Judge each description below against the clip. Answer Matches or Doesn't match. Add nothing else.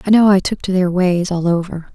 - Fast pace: Matches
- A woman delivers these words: Matches